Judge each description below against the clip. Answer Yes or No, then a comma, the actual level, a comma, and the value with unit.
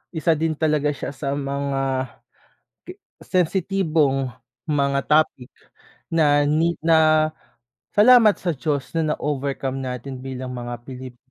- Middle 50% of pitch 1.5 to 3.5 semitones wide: Yes, average, 3.0 semitones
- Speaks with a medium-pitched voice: Yes, medium, 145 Hz